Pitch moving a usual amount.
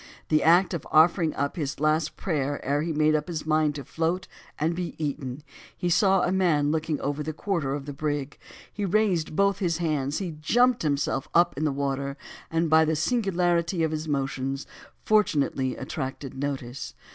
Yes: average, 3.3 semitones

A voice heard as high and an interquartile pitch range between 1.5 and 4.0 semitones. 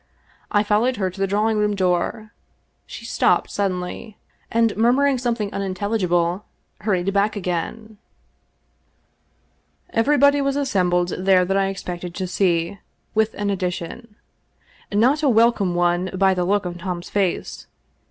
Yes: high, 200 Hz; average, 3.5 semitones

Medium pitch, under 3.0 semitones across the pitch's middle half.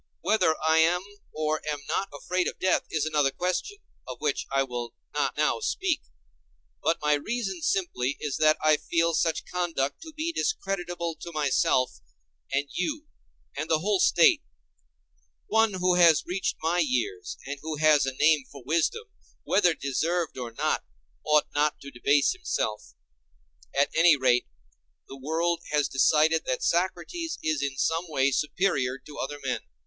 No: medium, 155 Hz; average, 4.1 semitones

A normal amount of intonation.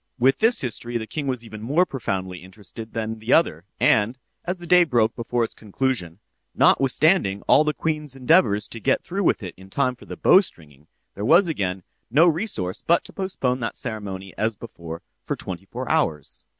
No: wide, 7.5 semitones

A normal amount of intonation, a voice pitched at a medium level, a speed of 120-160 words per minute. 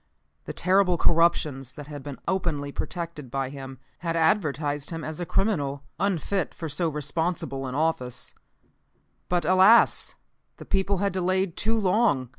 Yes: average, 4.6 semitones; medium, 165 Hz; average, 140 wpm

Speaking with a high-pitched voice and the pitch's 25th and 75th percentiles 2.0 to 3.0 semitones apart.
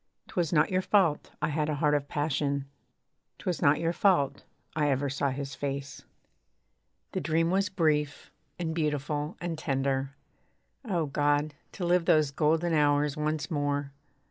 No: medium, 150 Hz; narrow, 2.5 semitones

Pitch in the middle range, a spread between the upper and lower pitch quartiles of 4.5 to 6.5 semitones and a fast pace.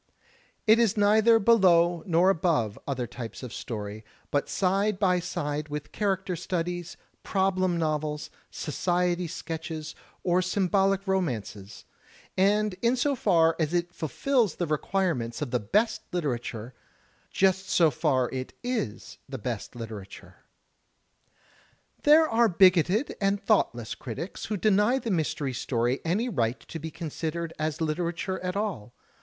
No: medium, 175 Hz; average, 5.1 semitones; slow, 135 wpm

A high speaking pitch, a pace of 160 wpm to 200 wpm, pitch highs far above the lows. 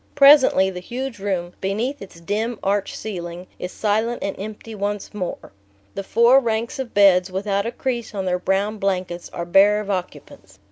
No: high, 200 Hz; average, 175 wpm; average, 3.3 semitones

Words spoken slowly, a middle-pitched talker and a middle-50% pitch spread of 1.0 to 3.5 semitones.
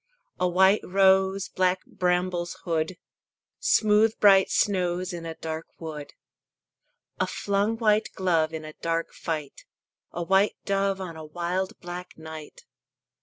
Yes: slow, 130 wpm; medium, 180 Hz; average, 2.8 semitones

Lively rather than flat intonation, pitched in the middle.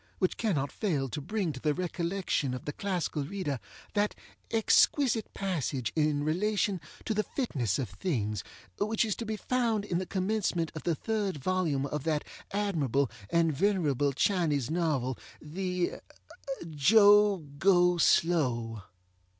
Yes: wide, 5.9 semitones; medium, 175 Hz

